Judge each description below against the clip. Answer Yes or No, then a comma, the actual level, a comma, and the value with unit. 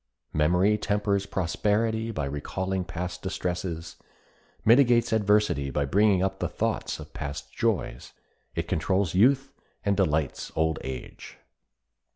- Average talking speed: No, slow, 120 wpm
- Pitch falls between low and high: No, very low, 95 Hz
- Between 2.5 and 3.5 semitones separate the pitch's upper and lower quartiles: No, average, 4.7 semitones